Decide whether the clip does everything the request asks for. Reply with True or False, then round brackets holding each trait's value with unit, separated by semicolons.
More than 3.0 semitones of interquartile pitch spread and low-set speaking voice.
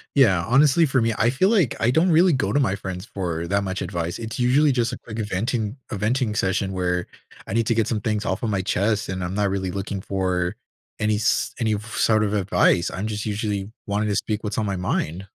True (3.4 semitones; 105 Hz)